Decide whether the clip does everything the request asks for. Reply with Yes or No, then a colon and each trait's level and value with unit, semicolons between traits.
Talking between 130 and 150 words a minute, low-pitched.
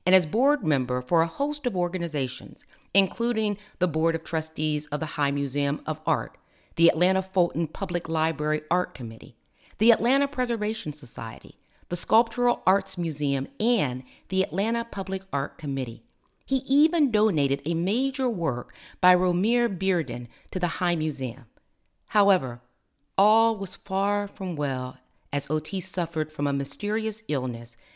No: average, 145 wpm; medium, 175 Hz